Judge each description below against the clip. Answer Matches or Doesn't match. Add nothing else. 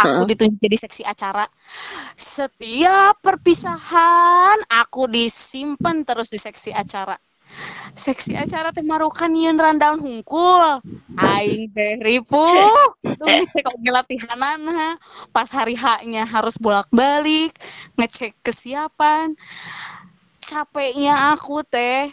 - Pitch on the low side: Doesn't match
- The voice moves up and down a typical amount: Doesn't match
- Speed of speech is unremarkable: Doesn't match